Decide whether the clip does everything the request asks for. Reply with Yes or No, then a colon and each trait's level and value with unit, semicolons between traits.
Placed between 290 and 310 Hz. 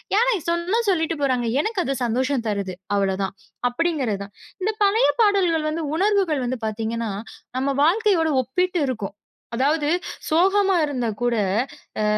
Yes: very high, 305 Hz